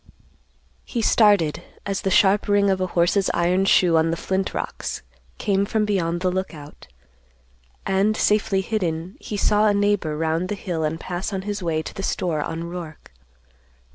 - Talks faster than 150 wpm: Yes, average, 170 wpm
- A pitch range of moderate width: Yes, average, 3.3 semitones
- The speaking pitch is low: No, high, 190 Hz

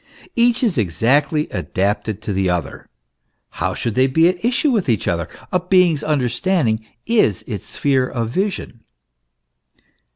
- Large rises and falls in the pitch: Yes, wide, 8.9 semitones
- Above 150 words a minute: No, average, 140 wpm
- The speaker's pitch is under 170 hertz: Yes, low, 135 Hz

